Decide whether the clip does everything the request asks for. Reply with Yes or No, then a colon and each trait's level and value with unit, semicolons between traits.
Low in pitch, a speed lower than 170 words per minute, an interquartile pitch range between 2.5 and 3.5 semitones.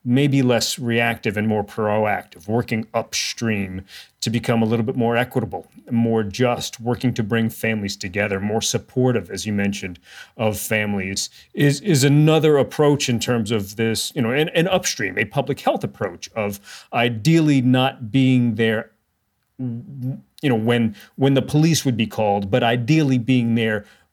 Yes: low, 115 Hz; average, 160 wpm; average, 3.1 semitones